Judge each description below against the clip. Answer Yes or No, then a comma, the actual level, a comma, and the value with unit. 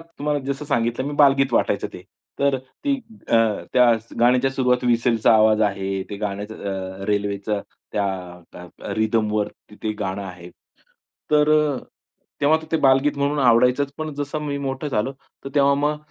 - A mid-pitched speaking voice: No, low, 125 Hz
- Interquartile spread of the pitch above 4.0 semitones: Yes, average, 5.2 semitones